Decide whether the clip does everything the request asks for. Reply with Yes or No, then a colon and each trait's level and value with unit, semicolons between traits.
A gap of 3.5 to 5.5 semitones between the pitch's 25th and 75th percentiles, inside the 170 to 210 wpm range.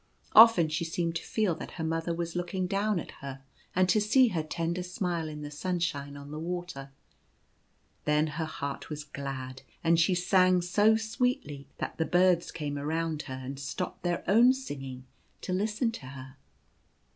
Yes: average, 4.0 semitones; average, 175 wpm